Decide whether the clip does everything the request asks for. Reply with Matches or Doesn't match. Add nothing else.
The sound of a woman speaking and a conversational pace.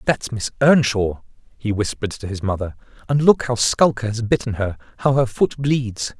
Doesn't match